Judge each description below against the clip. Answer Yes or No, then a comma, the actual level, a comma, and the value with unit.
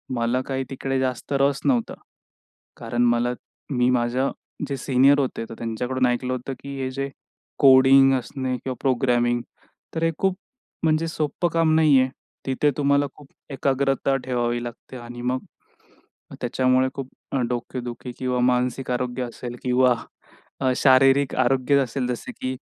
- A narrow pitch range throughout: Yes, narrow, 1.9 semitones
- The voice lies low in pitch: Yes, low, 130 Hz